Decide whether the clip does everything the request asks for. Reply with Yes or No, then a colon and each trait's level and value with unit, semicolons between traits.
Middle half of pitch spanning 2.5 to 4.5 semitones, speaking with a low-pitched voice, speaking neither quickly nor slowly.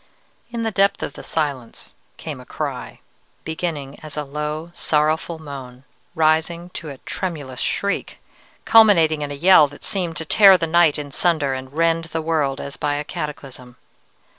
No: average, 3.0 semitones; medium, 155 Hz; average, 165 wpm